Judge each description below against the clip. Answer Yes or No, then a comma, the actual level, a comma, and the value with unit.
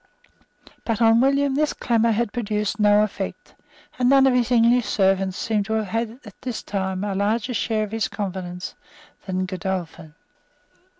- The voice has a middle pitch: No, high, 215 Hz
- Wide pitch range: No, average, 3.5 semitones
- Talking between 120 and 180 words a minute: Yes, average, 165 wpm